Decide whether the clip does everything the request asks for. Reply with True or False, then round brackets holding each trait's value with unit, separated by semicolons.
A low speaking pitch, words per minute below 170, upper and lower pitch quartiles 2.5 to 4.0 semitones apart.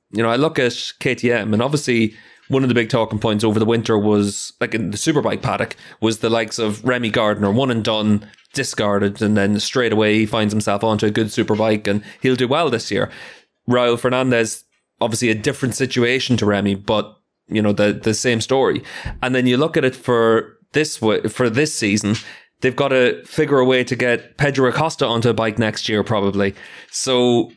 False (115 Hz; 205 wpm; 2.9 semitones)